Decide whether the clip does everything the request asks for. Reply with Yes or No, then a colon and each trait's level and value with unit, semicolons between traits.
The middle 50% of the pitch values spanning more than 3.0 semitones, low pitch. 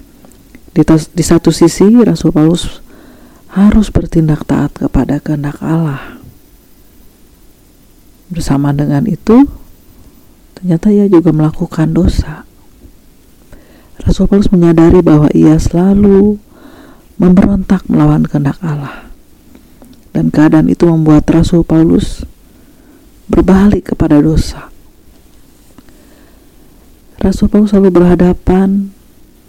No: average, 4.2 semitones; medium, 170 Hz